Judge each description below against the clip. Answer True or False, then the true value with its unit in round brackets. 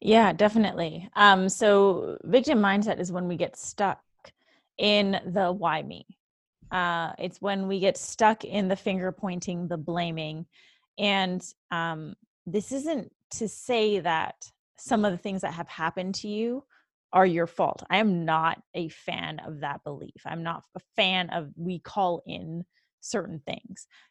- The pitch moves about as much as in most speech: True (3.3 semitones)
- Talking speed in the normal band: True (160 wpm)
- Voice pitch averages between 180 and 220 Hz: True (185 Hz)